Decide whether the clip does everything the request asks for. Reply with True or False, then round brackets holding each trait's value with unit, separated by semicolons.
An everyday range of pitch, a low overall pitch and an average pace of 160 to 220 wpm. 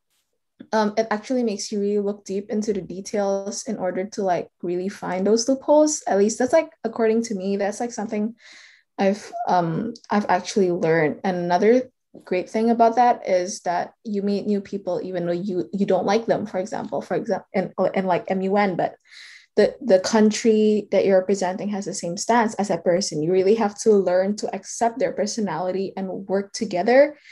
False (3.1 semitones; 200 Hz; 190 wpm)